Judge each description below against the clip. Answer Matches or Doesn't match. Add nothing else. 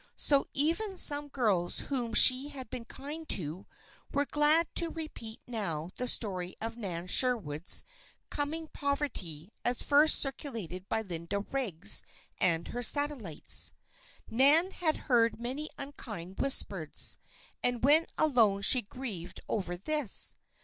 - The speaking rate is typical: Doesn't match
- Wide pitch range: Matches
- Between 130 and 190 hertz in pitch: Doesn't match